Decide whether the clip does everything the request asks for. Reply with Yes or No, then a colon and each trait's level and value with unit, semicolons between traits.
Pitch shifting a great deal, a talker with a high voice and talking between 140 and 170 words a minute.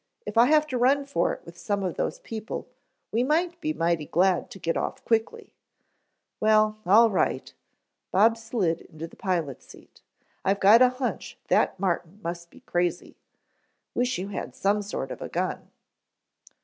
Yes: wide, 5.8 semitones; high, 205 Hz; average, 165 wpm